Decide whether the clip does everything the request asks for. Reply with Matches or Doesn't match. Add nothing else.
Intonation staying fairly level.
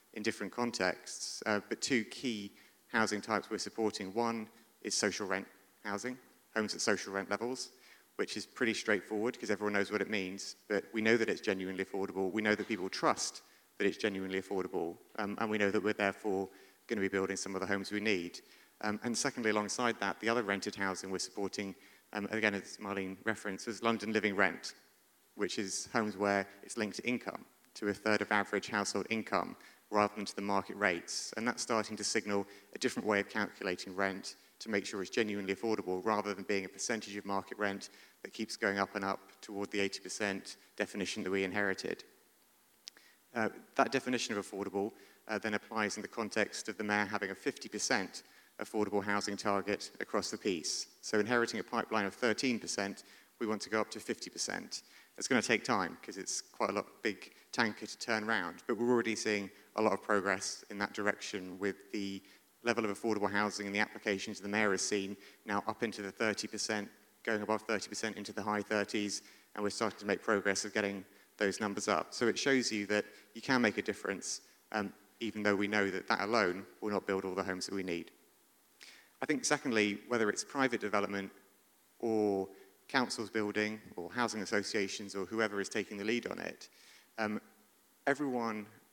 Matches